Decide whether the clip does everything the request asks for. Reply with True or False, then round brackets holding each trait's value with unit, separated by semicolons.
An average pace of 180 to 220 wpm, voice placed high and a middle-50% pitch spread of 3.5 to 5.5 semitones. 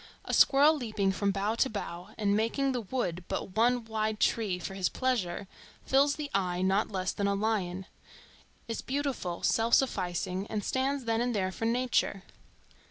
False (165 wpm; 215 Hz; 4.5 semitones)